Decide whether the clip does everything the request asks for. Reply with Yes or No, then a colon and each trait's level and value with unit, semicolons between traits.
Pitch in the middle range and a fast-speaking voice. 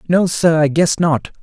Yes: medium, 160 Hz; fast, 210 wpm